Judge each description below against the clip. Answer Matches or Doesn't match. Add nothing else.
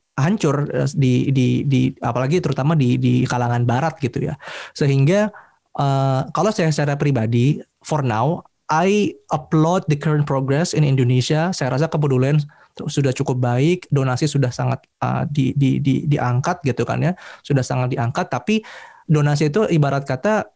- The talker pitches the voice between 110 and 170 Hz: Matches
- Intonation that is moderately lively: Matches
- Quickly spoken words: Matches